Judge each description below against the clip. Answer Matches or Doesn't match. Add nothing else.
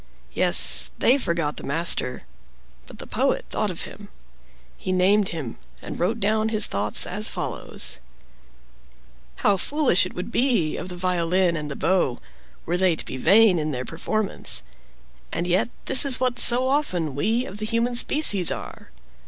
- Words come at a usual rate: Matches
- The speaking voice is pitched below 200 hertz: Matches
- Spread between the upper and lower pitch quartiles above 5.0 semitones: Matches